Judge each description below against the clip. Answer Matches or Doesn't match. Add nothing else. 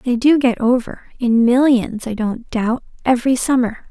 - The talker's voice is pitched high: Matches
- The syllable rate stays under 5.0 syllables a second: Matches